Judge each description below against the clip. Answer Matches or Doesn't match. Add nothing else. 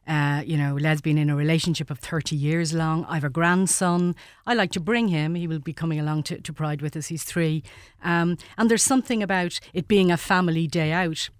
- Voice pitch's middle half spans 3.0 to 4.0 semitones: Doesn't match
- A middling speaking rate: Doesn't match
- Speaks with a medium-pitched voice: Matches